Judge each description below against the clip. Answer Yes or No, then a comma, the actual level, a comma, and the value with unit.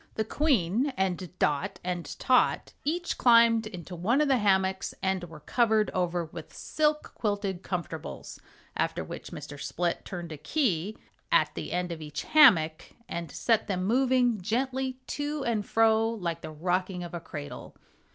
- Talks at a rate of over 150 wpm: Yes, average, 160 wpm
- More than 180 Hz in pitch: Yes, high, 190 Hz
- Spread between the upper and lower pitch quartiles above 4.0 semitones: Yes, wide, 5.5 semitones